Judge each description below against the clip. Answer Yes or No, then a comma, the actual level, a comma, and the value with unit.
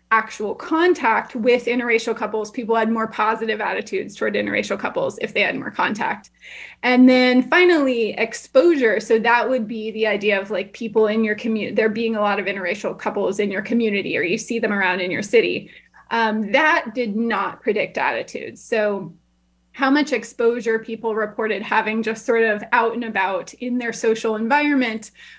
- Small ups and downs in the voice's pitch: Yes, narrow, 2.3 semitones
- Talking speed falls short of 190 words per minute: Yes, average, 175 wpm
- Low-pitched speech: No, high, 225 Hz